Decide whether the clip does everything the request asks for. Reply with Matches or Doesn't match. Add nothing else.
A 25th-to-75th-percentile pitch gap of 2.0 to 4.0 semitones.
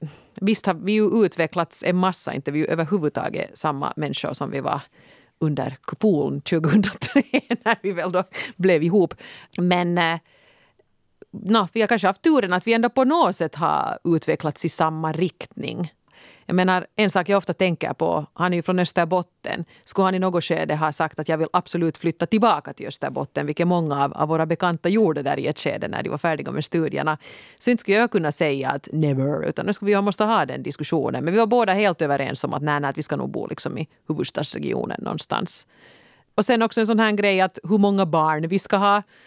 Doesn't match